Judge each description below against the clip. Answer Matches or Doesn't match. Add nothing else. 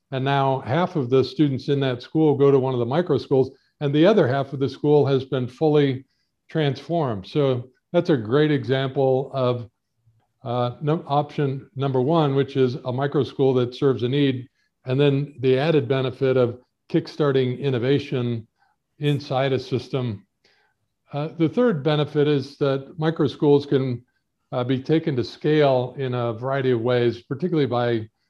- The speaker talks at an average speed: Matches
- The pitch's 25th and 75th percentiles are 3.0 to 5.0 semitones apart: Doesn't match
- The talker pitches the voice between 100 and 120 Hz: Doesn't match